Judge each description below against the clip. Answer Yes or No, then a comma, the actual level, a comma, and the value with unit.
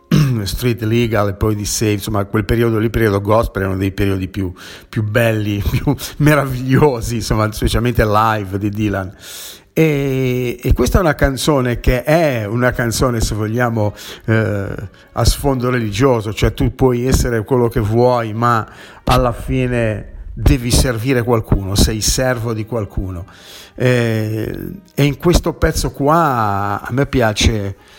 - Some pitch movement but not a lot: Yes, average, 3.2 semitones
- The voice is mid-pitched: No, low, 115 Hz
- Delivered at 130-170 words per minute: Yes, average, 145 wpm